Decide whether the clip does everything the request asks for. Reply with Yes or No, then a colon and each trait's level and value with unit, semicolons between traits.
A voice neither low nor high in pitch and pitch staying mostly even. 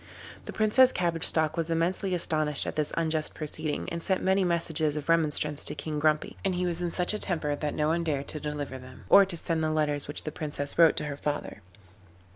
Yes: medium, 155 Hz; narrow, 2.3 semitones